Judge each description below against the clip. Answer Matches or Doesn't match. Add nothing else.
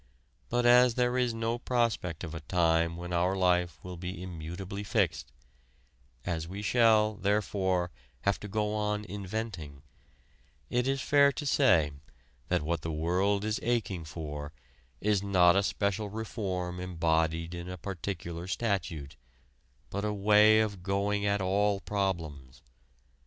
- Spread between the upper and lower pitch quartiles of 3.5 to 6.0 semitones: Matches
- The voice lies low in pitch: Matches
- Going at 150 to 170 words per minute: Doesn't match